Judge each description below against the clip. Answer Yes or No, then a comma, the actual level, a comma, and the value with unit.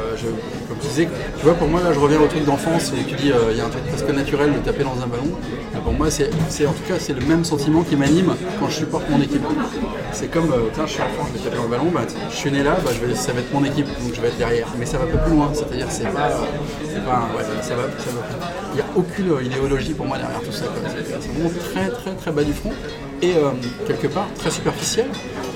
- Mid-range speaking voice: Yes, medium, 150 Hz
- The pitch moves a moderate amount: Yes, average, 3.1 semitones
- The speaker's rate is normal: No, fast, 265 wpm